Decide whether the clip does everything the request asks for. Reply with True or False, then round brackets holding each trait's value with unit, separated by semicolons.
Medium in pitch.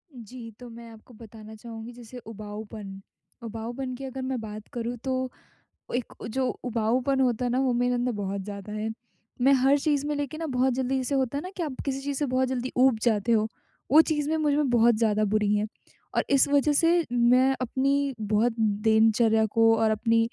False (245 Hz)